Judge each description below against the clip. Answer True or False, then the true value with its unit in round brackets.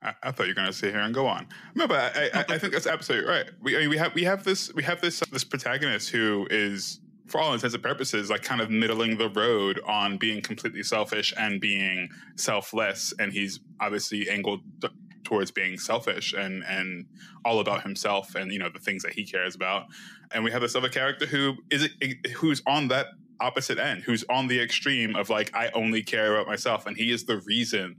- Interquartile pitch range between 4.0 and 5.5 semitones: True (4.4 semitones)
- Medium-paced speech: False (225 wpm)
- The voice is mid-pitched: False (110 Hz)